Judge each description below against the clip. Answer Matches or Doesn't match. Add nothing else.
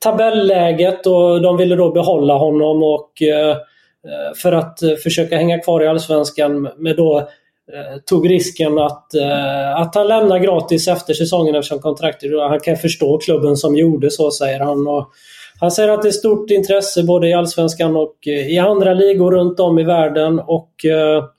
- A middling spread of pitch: Matches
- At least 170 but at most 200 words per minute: Doesn't match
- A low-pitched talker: Doesn't match